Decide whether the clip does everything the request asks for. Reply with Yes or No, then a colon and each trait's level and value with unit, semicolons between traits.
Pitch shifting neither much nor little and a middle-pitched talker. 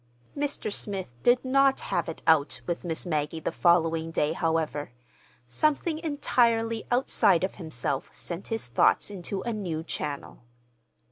No: wide, 6.4 semitones; medium, 175 Hz